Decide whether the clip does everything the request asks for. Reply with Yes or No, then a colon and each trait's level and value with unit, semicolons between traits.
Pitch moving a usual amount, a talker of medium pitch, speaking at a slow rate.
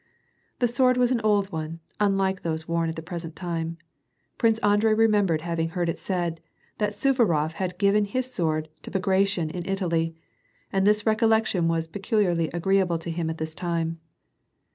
No: average, 4.0 semitones; medium, 180 Hz; average, 170 wpm